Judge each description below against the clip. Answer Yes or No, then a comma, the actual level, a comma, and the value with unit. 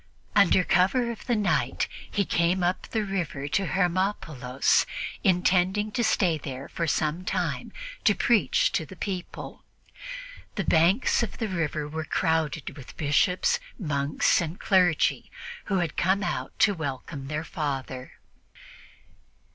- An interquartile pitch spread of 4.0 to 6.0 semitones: Yes, average, 4.4 semitones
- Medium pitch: Yes, medium, 175 Hz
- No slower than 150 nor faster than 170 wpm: No, slow, 135 wpm